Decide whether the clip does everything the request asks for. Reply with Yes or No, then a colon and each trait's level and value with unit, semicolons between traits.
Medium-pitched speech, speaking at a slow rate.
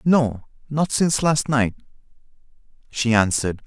No: low, 130 Hz; slow, 100 wpm